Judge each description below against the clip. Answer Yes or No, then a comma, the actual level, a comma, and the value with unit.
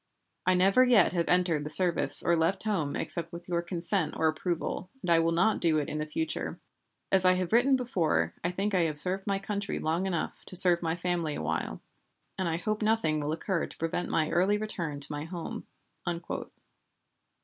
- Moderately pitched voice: Yes, medium, 175 Hz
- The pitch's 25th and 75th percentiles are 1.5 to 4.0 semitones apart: Yes, average, 3.1 semitones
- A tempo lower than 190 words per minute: No, average, 200 wpm